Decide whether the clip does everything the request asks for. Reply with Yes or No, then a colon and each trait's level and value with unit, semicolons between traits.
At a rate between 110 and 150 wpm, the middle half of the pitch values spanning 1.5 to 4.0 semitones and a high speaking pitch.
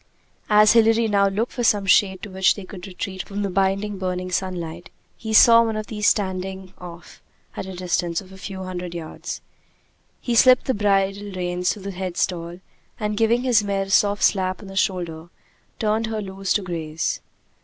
No: average, 190 wpm; narrow, 2.4 semitones; high, 195 Hz